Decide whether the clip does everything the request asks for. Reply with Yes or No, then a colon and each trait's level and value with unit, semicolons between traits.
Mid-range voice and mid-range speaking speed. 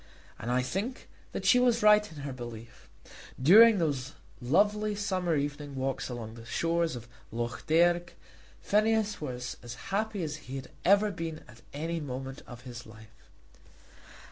Yes: medium, 150 Hz; average, 155 wpm